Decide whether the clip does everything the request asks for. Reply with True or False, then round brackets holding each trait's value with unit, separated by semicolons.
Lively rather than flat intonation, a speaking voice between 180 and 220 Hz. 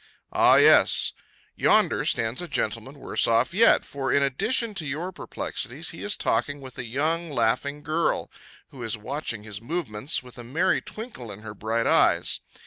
False (5.7 semitones; 135 Hz)